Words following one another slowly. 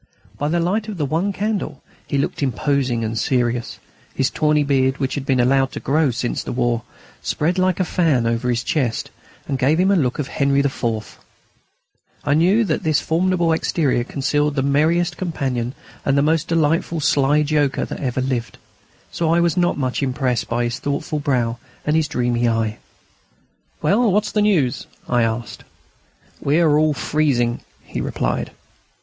No: average, 175 wpm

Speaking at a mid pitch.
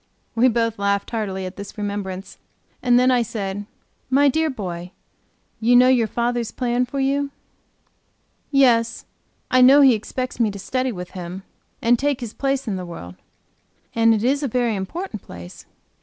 No: high, 230 Hz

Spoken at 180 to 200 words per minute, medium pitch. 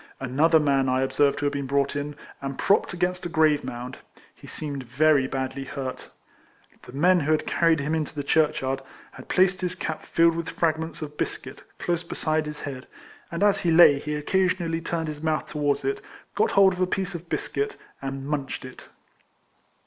Yes: average, 195 wpm; medium, 155 Hz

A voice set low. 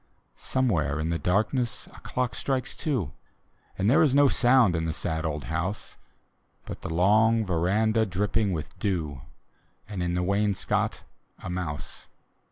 Yes: very low, 95 Hz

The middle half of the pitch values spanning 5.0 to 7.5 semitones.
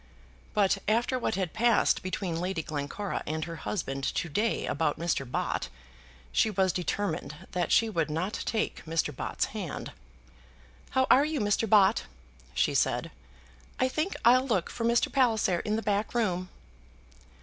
Yes: wide, 5.4 semitones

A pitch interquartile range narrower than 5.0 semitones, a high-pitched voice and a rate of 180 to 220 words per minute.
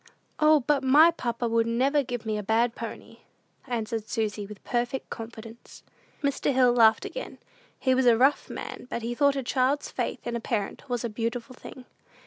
Yes: average, 2.7 semitones; high, 240 Hz; average, 185 wpm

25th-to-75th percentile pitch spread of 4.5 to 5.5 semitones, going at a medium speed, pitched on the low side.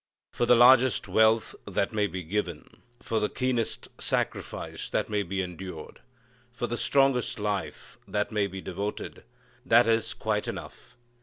No: average, 3.3 semitones; average, 150 wpm; low, 105 Hz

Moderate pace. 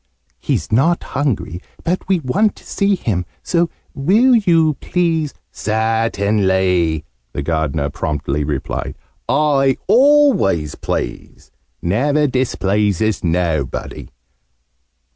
No: slow, 100 wpm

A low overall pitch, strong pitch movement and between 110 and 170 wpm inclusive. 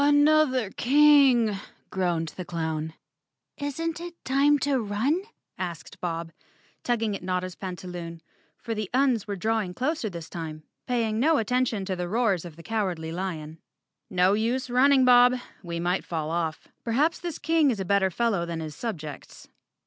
No: high, 205 Hz; wide, 6.9 semitones; average, 155 wpm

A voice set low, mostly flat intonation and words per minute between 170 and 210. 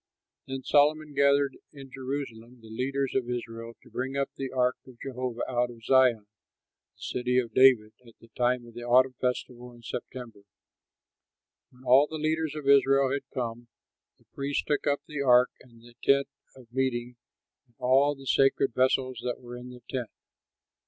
Yes: low, 130 Hz; narrow, 2.2 semitones; average, 175 wpm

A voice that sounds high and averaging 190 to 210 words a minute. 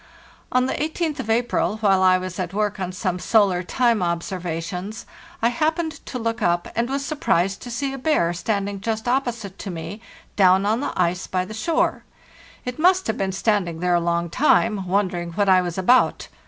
Yes: high, 200 Hz; average, 195 wpm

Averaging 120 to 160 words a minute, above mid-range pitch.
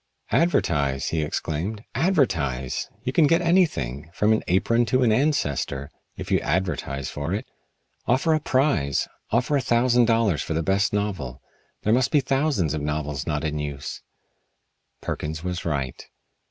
No: average, 155 wpm; very low, 95 Hz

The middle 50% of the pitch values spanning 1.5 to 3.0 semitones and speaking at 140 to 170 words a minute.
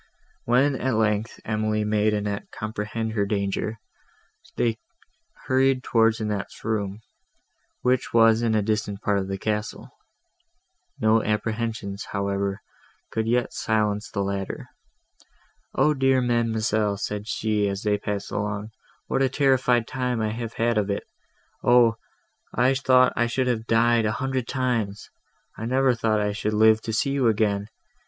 Yes: narrow, 2.4 semitones; average, 145 wpm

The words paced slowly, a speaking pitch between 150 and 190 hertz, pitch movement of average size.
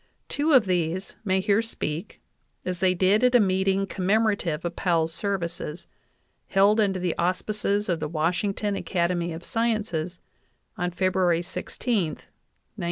No: average, 150 wpm; medium, 185 Hz; average, 3.0 semitones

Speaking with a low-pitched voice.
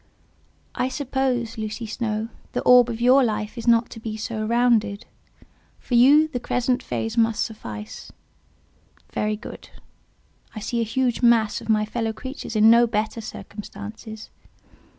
No: high, 230 Hz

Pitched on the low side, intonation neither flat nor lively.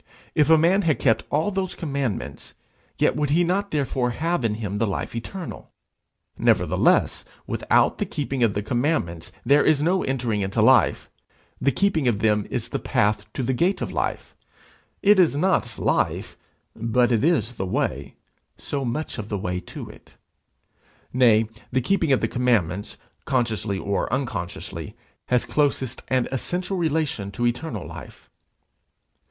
No: low, 125 Hz; wide, 6.5 semitones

